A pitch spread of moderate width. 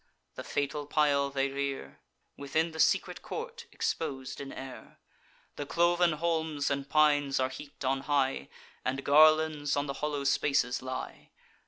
No: narrow, 2.3 semitones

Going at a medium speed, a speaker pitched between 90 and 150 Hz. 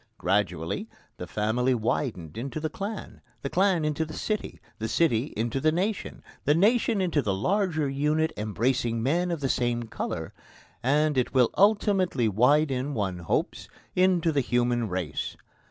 Yes: average, 155 wpm; medium, 140 Hz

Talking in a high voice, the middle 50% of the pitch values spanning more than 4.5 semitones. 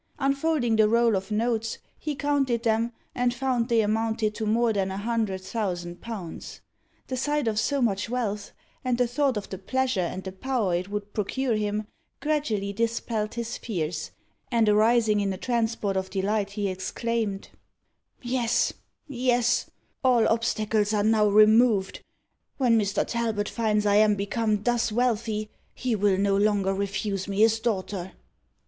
No: high, 220 Hz; average, 2.9 semitones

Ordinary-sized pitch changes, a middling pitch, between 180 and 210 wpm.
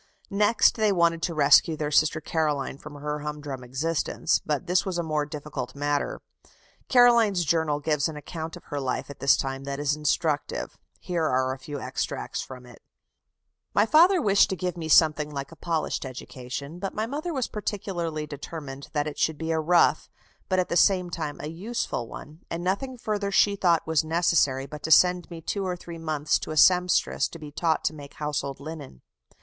Yes: average, 3.5 semitones; medium, 160 Hz; average, 195 wpm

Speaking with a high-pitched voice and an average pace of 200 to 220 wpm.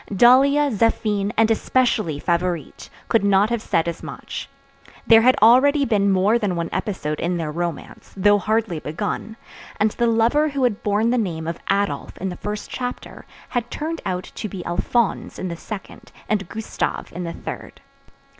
No: high, 210 Hz; average, 175 wpm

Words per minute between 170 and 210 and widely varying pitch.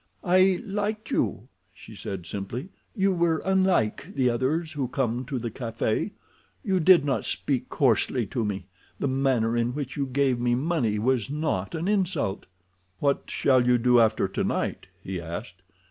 No: average, 160 wpm; wide, 6.2 semitones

